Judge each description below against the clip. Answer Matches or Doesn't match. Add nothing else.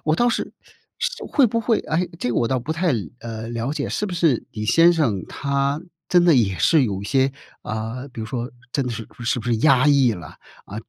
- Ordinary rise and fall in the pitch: Doesn't match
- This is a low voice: Matches